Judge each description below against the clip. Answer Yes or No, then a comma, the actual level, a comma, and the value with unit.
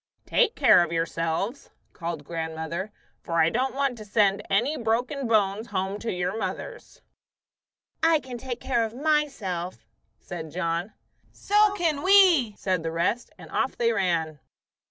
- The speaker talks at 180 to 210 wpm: No, average, 150 wpm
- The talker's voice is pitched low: No, high, 210 Hz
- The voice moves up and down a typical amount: No, wide, 7.5 semitones